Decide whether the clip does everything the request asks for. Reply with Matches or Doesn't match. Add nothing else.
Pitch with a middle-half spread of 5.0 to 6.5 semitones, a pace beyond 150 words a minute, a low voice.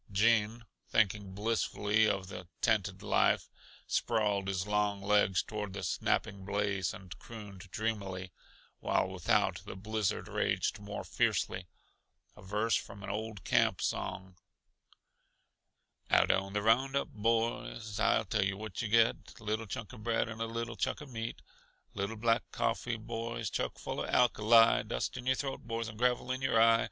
Doesn't match